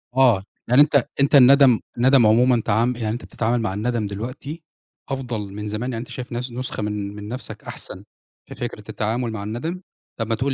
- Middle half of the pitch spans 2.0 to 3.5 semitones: Yes, average, 3.2 semitones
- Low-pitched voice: Yes, low, 120 Hz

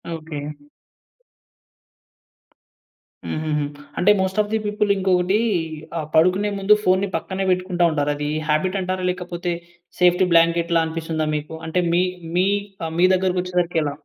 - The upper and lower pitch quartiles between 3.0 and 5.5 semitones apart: No, narrow, 2.6 semitones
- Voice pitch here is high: No, medium, 180 Hz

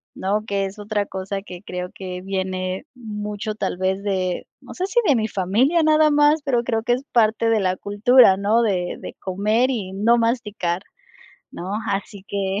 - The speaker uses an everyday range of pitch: Yes, average, 3.5 semitones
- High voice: Yes, high, 205 Hz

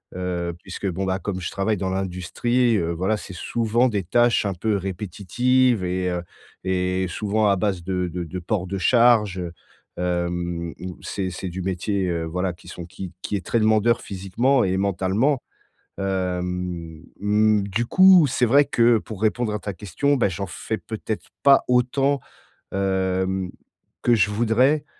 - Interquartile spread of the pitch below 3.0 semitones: No, average, 3.6 semitones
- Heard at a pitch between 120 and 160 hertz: No, very low, 95 Hz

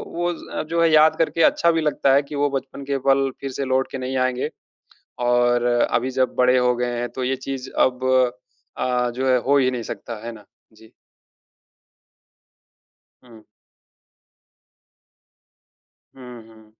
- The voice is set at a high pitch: No, low, 130 Hz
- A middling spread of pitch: No, narrow, 2.1 semitones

